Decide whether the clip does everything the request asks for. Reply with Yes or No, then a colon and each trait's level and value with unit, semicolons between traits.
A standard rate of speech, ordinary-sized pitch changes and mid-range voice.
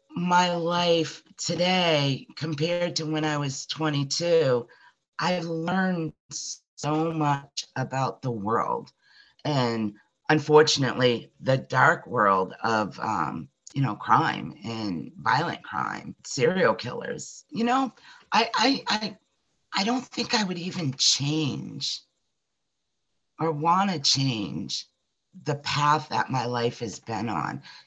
No: slow, 120 wpm; average, 5.0 semitones; medium, 155 Hz